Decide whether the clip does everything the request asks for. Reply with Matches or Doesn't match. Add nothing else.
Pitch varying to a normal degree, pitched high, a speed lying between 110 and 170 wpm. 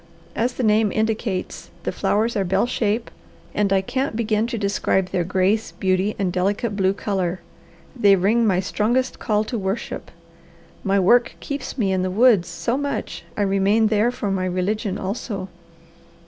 Matches